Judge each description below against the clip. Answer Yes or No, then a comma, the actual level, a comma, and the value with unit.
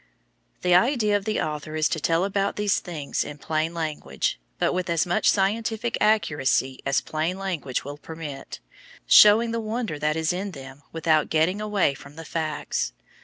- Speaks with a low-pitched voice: No, medium, 165 Hz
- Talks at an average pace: Yes, average, 170 wpm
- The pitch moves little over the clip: No, average, 5.1 semitones